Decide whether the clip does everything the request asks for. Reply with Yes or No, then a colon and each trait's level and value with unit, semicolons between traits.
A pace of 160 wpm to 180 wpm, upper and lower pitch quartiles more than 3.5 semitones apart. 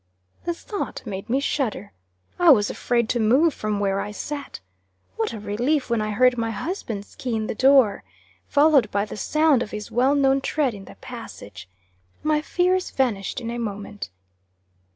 Yes: average, 175 wpm; average, 5.1 semitones